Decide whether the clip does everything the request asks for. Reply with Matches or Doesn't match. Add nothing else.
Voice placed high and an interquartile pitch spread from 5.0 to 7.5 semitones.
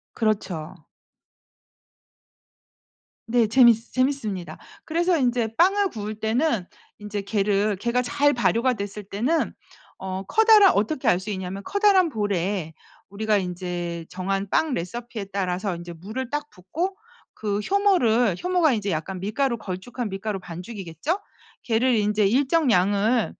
Matches